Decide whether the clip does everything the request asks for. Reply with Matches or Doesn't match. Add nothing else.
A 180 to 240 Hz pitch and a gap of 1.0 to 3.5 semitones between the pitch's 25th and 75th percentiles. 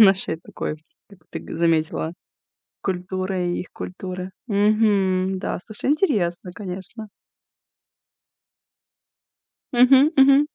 Matches